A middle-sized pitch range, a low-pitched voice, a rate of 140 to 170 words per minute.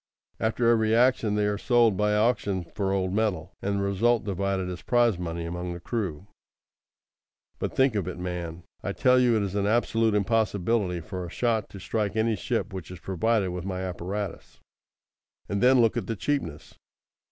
No: average, 3.7 semitones; low, 100 Hz; average, 185 wpm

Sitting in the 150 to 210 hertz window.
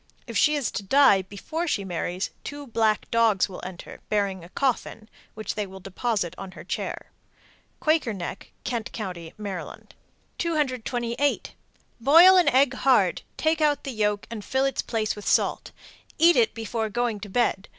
No: high, 225 Hz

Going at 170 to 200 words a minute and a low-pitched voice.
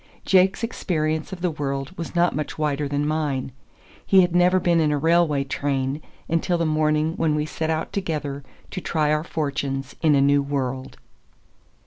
No: average, 175 wpm; medium, 155 Hz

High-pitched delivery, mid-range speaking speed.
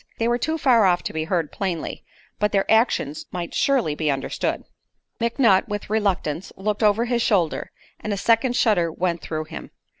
Yes: high, 200 Hz; average, 180 wpm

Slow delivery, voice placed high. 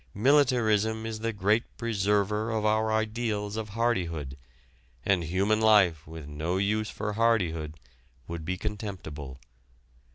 No: slow, 125 wpm; low, 105 Hz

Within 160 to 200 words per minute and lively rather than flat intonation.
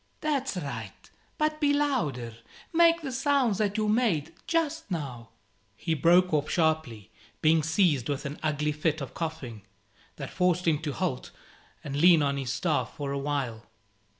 Yes: average, 165 wpm; wide, 6.8 semitones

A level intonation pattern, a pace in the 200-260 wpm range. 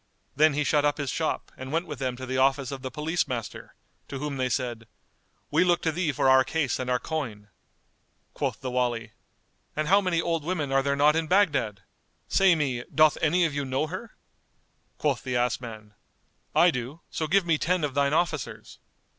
No: average, 3.9 semitones; fast, 205 wpm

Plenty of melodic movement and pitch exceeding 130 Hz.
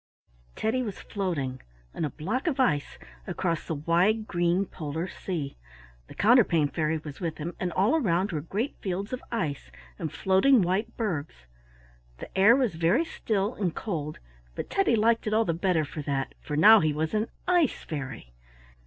Yes: wide, 5.9 semitones; medium, 185 Hz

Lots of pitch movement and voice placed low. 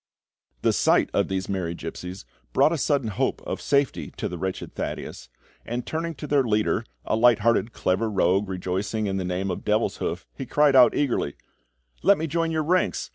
Yes: wide, 7.3 semitones; low, 110 Hz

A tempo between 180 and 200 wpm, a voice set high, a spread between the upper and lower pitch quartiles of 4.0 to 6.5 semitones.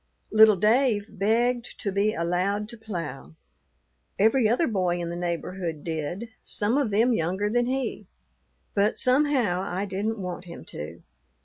No: average, 145 wpm; high, 205 Hz; average, 4.4 semitones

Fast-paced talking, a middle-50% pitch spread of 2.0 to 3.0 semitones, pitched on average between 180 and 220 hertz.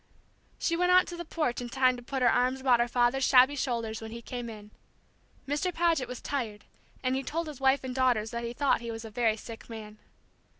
No: fast, 230 wpm; average, 2.7 semitones; very high, 250 Hz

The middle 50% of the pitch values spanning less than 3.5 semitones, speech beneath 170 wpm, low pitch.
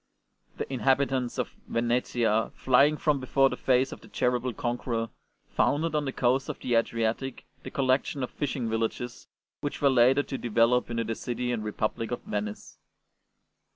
Yes: narrow, 2.5 semitones; average, 160 wpm; low, 125 Hz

